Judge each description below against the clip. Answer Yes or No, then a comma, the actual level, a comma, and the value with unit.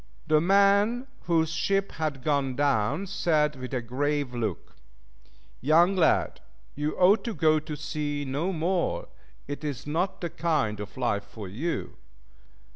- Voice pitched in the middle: Yes, medium, 150 Hz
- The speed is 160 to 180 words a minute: No, average, 145 wpm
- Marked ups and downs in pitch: No, average, 4.1 semitones